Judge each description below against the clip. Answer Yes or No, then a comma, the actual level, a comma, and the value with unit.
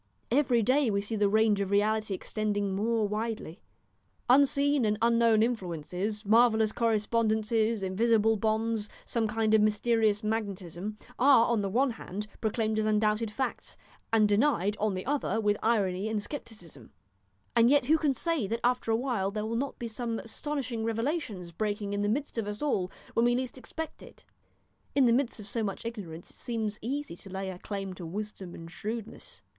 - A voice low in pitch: No, high, 220 Hz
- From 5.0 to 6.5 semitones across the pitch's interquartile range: No, narrow, 2.4 semitones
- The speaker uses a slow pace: No, average, 180 wpm